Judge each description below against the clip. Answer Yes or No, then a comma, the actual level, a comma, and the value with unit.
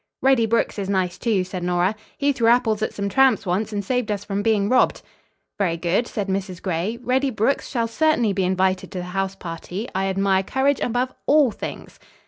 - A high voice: Yes, high, 205 Hz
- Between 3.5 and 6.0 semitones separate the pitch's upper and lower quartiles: Yes, average, 4.1 semitones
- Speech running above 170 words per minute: Yes, average, 200 wpm